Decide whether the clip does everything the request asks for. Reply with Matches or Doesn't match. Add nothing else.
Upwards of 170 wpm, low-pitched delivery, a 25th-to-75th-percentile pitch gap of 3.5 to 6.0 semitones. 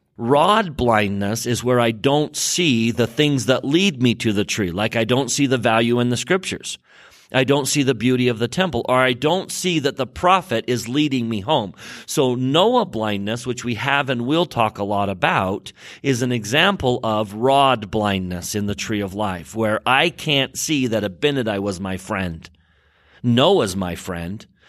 Matches